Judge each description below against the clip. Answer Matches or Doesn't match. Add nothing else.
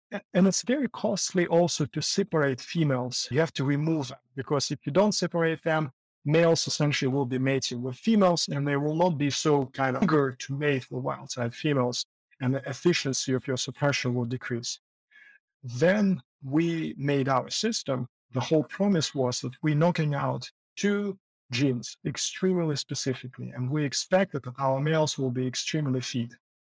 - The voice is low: Doesn't match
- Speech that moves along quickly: Doesn't match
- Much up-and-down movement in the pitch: Doesn't match